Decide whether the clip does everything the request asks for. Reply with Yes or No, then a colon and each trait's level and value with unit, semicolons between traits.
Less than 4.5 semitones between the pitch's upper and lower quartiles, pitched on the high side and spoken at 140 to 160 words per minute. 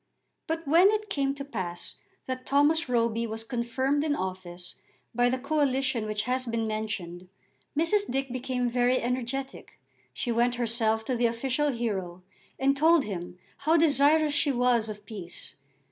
Yes: average, 4.0 semitones; high, 245 Hz; average, 155 wpm